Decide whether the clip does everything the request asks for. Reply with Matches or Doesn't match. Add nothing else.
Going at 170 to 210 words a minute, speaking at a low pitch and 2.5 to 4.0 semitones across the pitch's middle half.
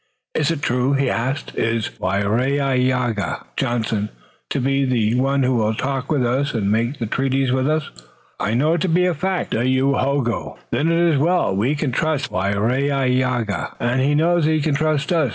Matches